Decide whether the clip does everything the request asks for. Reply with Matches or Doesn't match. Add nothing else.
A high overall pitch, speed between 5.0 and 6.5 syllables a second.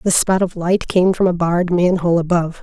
Doesn't match